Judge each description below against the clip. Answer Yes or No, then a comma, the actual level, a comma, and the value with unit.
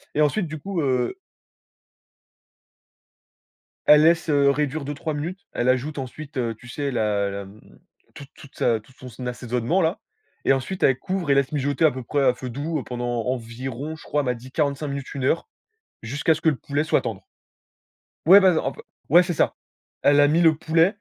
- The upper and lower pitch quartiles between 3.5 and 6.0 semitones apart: Yes, average, 3.9 semitones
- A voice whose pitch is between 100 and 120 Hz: No, medium, 140 Hz